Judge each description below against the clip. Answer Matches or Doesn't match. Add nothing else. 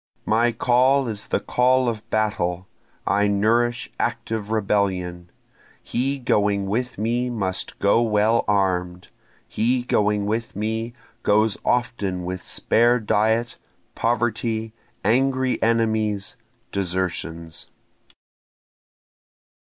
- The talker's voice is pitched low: Matches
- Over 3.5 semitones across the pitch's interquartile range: Doesn't match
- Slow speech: Matches